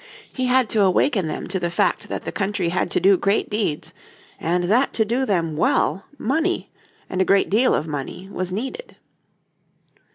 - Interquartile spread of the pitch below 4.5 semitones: No, average, 5.1 semitones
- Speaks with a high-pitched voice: Yes, high, 195 Hz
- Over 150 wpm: Yes, average, 185 wpm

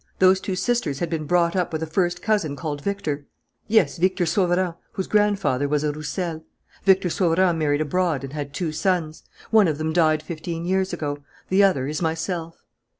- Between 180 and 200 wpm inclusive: Yes, average, 185 wpm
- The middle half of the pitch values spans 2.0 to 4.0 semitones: Yes, average, 3.3 semitones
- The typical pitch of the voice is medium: Yes, medium, 170 Hz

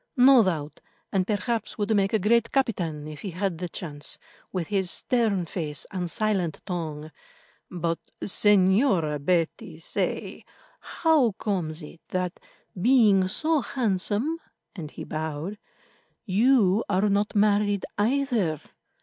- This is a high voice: Yes, high, 195 Hz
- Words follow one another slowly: Yes, slow, 125 wpm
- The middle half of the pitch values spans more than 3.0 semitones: Yes, average, 4.6 semitones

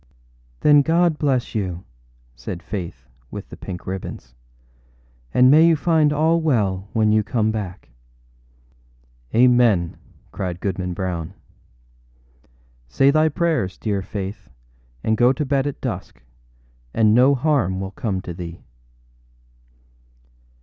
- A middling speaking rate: No, slow, 125 wpm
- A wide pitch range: Yes, wide, 7.6 semitones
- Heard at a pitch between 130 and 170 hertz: No, low, 105 Hz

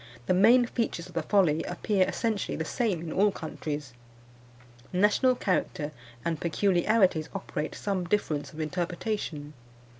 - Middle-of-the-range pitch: Yes, medium, 180 Hz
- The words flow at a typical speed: No, slow, 130 wpm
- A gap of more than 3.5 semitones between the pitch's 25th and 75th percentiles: Yes, average, 4.8 semitones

